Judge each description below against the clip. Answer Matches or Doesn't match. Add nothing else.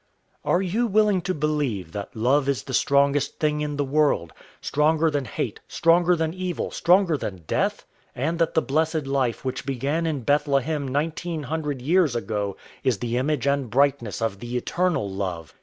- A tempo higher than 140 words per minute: Matches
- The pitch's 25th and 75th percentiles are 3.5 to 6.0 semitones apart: Matches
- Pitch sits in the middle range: Matches